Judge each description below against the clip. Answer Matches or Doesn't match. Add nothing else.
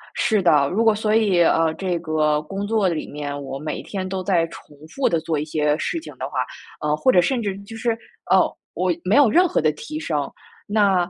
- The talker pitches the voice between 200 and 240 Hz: Doesn't match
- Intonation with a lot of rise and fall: Matches